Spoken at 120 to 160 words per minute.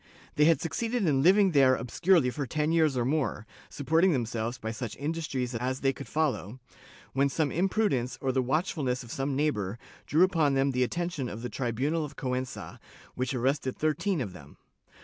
No: average, 190 wpm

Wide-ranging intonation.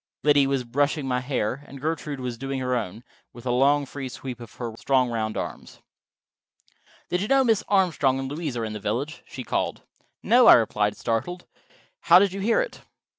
No: average, 4.4 semitones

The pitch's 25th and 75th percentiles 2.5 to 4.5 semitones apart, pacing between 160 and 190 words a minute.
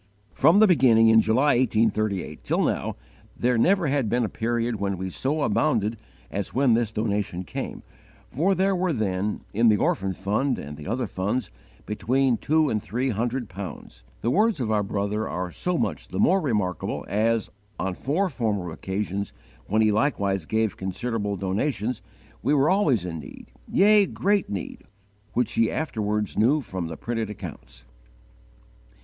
No: average, 5.0 semitones; average, 165 wpm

